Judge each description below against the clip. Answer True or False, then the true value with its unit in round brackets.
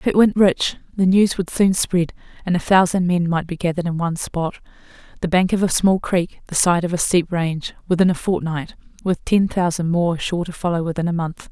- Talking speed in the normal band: False (220 wpm)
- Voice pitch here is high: False (175 Hz)